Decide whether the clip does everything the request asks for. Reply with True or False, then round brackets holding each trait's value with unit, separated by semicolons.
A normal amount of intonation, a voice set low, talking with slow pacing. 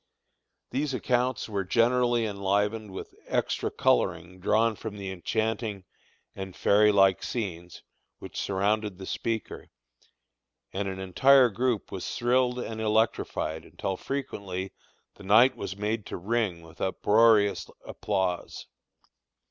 True (3.3 semitones; 105 Hz; 120 wpm)